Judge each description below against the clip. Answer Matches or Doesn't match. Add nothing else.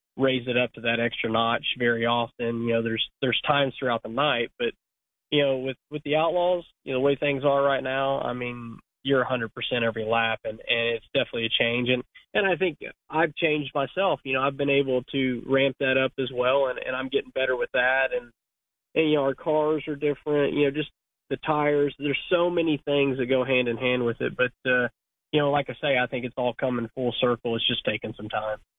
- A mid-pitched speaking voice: Doesn't match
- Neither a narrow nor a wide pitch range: Matches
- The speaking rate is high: Matches